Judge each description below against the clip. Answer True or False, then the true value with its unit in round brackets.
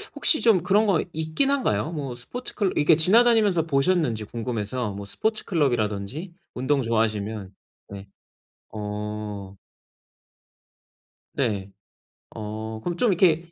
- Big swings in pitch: True (8.8 semitones)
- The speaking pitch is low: True (130 Hz)